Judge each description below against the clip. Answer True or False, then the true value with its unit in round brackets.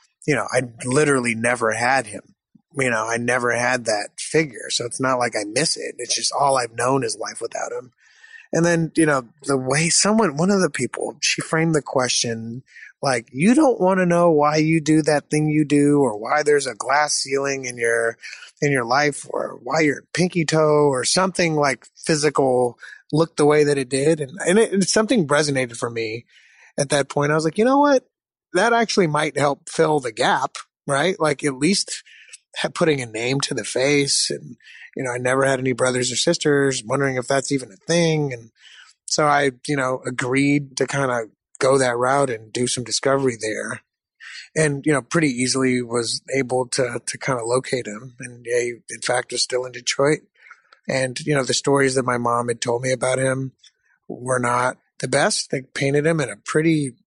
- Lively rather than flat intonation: False (3.7 semitones)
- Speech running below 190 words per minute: False (205 wpm)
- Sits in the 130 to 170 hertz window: True (140 Hz)